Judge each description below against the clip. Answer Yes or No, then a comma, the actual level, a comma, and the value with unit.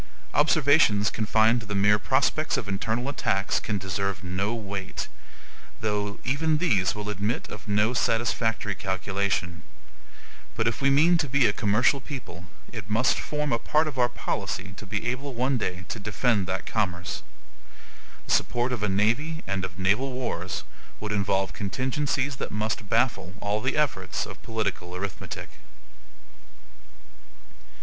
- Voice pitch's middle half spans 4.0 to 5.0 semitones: Yes, average, 4.5 semitones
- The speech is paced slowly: No, average, 150 wpm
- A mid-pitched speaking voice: No, low, 110 Hz